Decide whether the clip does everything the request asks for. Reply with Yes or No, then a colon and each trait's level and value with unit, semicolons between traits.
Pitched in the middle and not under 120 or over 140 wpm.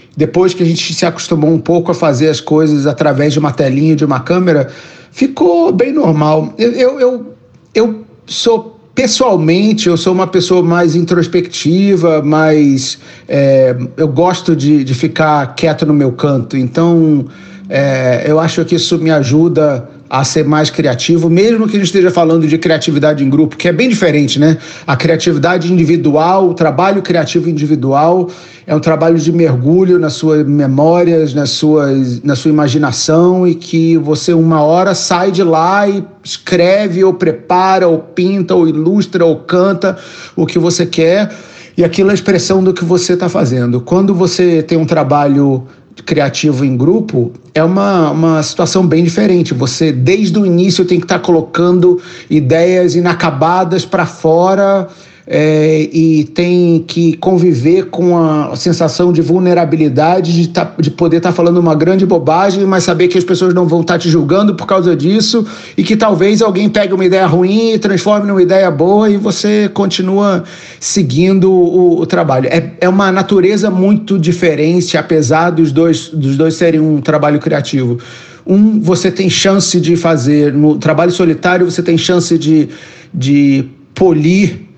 No: medium, 170 Hz; average, 165 wpm